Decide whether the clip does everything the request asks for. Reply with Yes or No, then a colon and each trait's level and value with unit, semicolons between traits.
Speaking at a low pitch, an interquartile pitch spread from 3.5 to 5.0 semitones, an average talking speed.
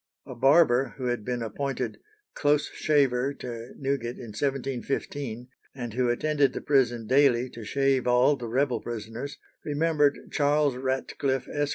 No: low, 130 Hz; average, 2.8 semitones; average, 145 wpm